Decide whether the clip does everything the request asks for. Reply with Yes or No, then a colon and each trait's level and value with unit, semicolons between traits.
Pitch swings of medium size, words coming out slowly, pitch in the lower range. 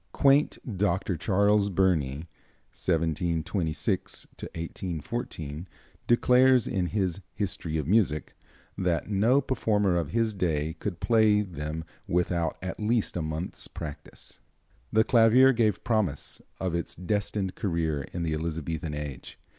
Yes: average, 4.7 semitones; slow, 120 wpm; very low, 90 Hz